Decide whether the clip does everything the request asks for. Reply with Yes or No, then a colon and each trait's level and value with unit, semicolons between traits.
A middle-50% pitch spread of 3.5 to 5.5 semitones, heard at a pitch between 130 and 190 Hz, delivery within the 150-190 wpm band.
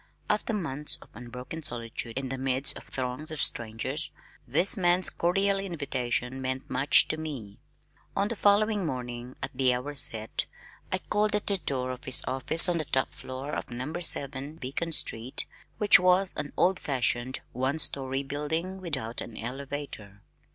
Yes: average, 5.2 semitones; medium, 140 Hz; average, 165 wpm